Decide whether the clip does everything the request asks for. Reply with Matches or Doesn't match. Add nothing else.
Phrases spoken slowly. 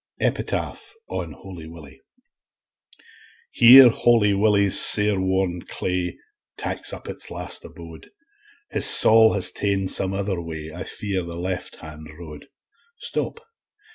Matches